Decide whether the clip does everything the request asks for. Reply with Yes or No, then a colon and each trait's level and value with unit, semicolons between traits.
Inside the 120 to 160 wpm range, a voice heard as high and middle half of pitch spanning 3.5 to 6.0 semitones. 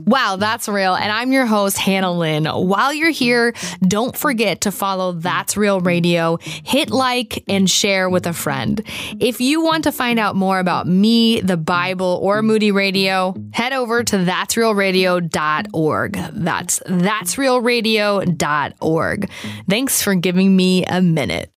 Yes: average, 150 wpm; high, 195 Hz; average, 4.1 semitones